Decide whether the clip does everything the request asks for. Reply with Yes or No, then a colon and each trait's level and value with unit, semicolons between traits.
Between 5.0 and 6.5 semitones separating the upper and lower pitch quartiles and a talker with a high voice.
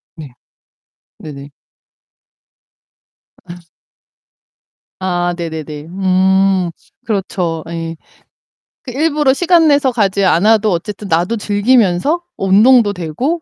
Yes: wide, 5.6 semitones; high, 195 Hz